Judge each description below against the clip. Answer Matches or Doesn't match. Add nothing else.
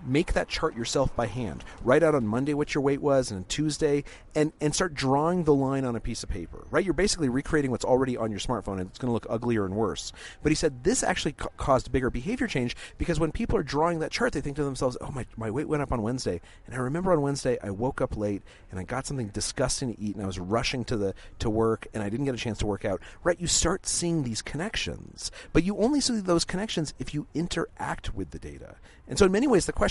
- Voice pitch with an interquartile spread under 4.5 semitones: Doesn't match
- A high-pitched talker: Doesn't match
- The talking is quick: Matches